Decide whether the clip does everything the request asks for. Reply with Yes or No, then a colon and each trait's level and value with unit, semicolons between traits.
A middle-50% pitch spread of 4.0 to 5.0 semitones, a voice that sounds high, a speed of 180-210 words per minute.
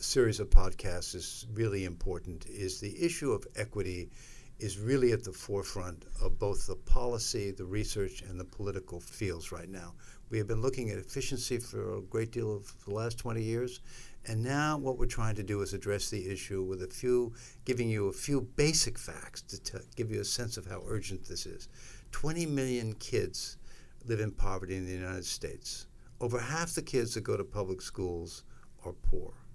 No: average, 4.5 semitones; low, 105 Hz; average, 195 wpm